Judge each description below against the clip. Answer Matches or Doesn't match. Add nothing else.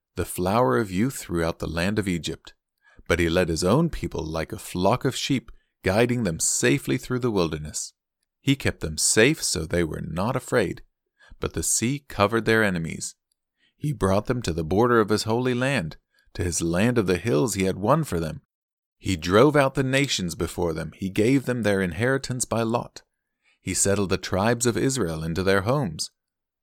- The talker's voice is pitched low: Matches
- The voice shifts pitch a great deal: Matches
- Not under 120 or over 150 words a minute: Doesn't match